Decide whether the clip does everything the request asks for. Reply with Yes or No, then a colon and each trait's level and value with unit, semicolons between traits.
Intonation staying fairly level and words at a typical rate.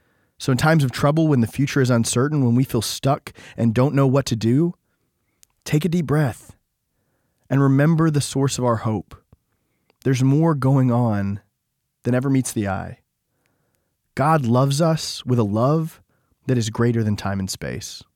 No: average, 3.7 semitones; average, 175 wpm